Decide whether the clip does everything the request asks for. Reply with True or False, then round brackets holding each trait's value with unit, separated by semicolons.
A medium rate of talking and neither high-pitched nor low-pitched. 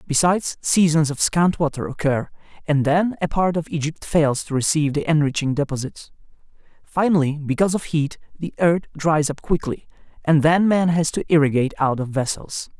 True (170 wpm; 155 Hz)